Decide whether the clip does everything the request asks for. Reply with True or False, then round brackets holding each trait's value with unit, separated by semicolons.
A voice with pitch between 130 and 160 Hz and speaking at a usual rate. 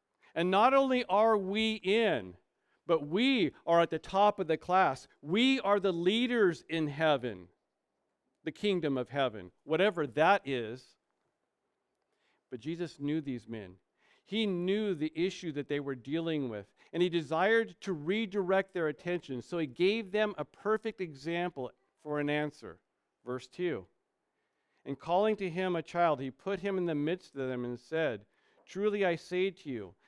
False (170 Hz; 165 wpm)